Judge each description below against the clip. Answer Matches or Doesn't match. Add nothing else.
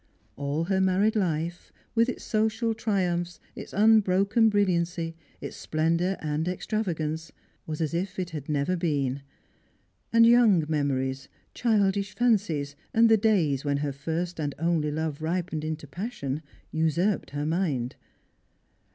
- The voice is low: Doesn't match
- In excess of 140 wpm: Doesn't match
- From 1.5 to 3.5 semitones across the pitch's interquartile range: Doesn't match